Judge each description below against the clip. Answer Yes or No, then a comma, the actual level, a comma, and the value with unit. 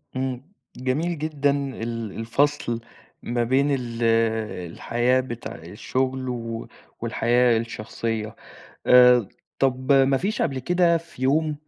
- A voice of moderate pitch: No, low, 130 Hz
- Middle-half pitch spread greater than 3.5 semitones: No, average, 3.1 semitones